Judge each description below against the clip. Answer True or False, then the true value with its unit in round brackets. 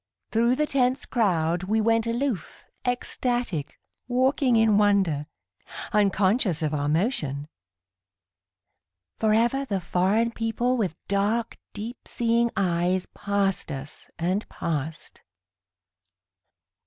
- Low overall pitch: False (210 Hz)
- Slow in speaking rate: True (100 wpm)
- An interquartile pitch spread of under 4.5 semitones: False (5.0 semitones)